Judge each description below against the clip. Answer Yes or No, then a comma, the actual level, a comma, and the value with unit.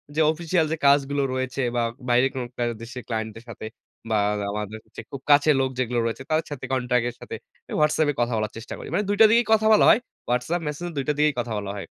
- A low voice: Yes, low, 130 Hz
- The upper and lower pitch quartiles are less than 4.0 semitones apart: No, average, 4.4 semitones